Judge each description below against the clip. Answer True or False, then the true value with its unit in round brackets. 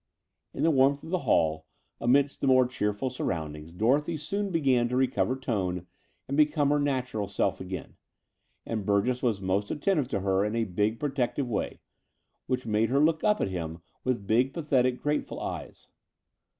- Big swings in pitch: True (5.8 semitones)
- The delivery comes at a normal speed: True (170 wpm)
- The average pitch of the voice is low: True (125 Hz)